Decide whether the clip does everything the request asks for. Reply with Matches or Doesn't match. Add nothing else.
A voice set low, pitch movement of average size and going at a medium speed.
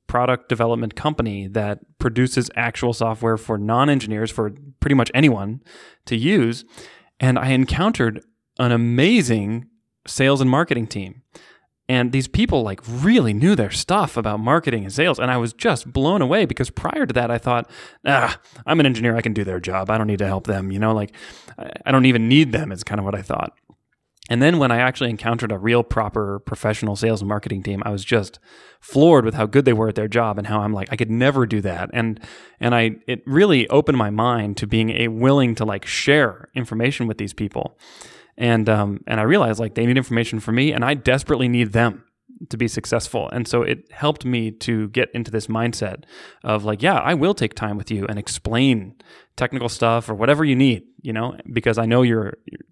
Doesn't match